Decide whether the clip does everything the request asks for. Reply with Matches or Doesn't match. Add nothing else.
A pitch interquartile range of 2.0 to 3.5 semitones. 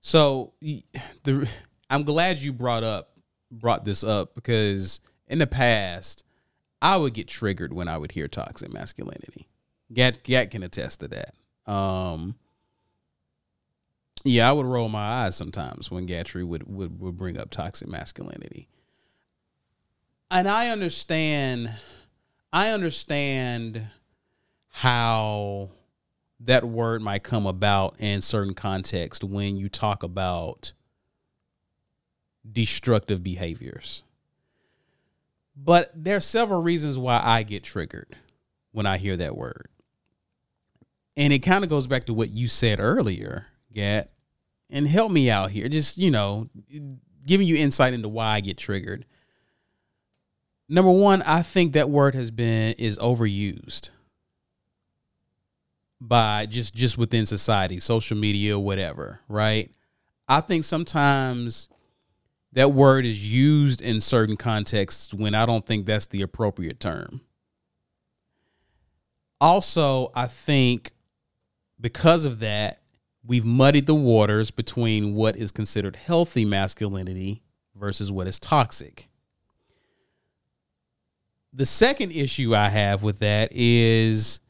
Doesn't match